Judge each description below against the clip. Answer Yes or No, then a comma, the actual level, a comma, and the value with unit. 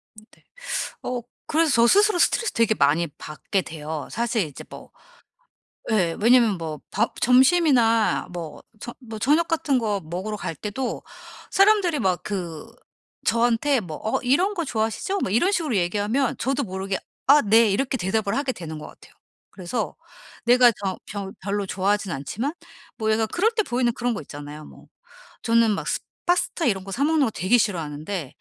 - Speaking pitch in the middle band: No, high, 220 Hz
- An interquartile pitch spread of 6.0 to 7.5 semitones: No, wide, 5.6 semitones